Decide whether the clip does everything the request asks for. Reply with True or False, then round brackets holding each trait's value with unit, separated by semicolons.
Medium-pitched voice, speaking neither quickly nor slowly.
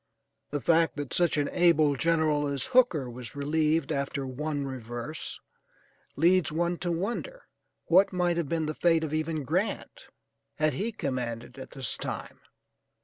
True (155 Hz; 150 wpm)